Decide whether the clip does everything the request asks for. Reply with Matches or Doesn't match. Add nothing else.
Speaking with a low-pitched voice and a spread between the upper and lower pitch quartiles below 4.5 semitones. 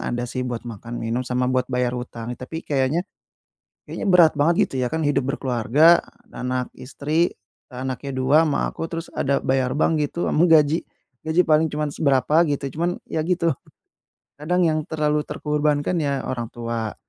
Doesn't match